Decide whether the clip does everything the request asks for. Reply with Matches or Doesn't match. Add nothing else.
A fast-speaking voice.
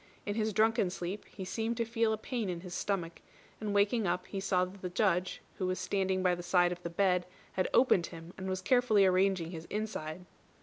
Matches